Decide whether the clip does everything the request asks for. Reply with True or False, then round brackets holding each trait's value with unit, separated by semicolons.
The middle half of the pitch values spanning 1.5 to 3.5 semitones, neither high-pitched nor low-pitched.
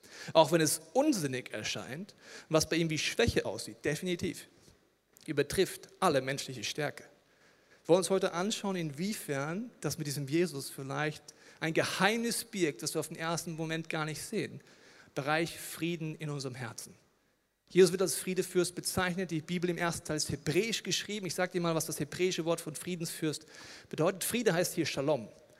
True (3.1 semitones; 165 Hz)